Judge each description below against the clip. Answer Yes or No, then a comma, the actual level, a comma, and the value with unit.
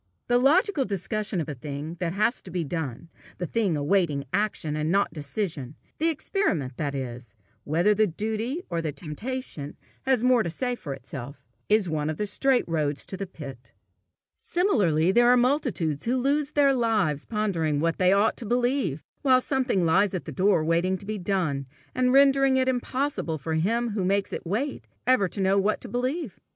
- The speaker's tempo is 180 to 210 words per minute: Yes, average, 190 wpm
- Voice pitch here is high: Yes, high, 195 Hz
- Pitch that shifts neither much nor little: No, wide, 7.7 semitones